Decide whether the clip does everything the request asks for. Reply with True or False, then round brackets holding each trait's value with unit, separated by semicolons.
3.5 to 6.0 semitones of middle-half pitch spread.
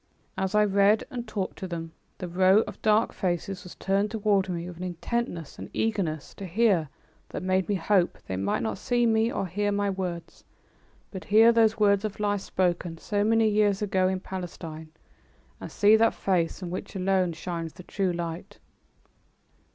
False (3.1 semitones)